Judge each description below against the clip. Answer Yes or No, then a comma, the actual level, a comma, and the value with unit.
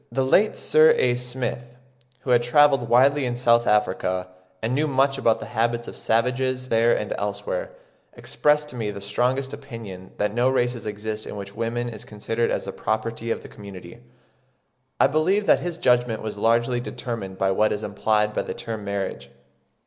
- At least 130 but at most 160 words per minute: No, average, 180 wpm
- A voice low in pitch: Yes, low, 120 Hz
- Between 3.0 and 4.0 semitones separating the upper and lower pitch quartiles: Yes, average, 3.4 semitones